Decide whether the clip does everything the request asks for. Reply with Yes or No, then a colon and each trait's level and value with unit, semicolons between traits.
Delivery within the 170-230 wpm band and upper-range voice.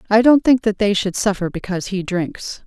Yes: average, 200 wpm; high, 205 Hz